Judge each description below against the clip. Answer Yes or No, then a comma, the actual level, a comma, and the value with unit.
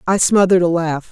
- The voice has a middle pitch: Yes, medium, 175 Hz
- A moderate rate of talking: No, fast, 215 wpm